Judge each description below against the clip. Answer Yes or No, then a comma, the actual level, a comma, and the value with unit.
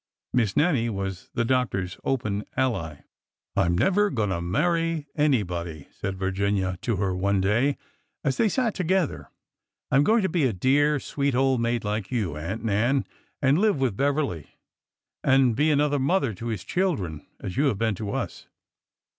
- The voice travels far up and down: Yes, wide, 6.8 semitones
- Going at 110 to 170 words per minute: No, average, 180 wpm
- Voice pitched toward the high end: No, low, 120 Hz